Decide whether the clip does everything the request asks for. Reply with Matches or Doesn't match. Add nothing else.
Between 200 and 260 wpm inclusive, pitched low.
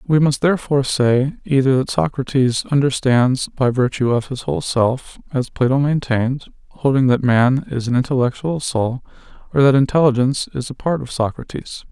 Doesn't match